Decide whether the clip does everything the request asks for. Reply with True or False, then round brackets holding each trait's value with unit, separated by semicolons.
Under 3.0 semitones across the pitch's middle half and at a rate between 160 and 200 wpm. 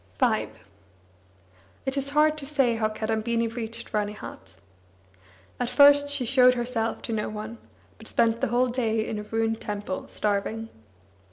False (2.6 semitones; 150 wpm)